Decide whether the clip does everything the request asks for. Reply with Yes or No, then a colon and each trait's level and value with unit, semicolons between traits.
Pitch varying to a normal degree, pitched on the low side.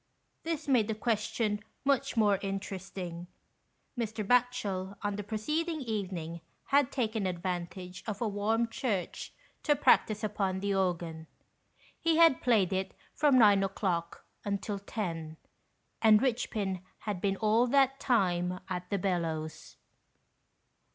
No: average, 3.9 semitones; high, 205 Hz